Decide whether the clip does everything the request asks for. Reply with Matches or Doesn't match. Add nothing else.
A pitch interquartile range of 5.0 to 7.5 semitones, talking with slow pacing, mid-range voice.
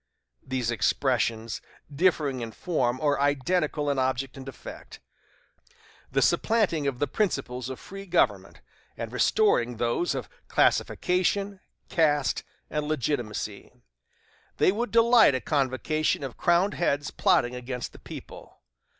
Matches